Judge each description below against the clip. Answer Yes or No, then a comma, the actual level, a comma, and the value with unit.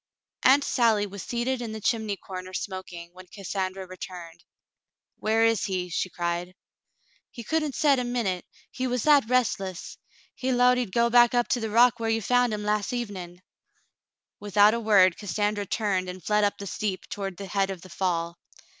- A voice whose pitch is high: Yes, high, 205 Hz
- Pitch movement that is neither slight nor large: Yes, average, 4.3 semitones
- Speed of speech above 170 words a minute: Yes, average, 180 wpm